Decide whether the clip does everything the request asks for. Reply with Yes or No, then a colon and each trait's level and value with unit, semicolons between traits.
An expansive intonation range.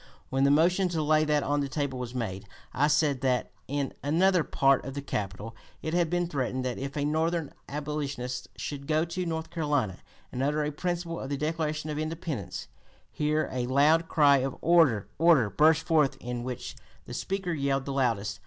No: average, 3.4 semitones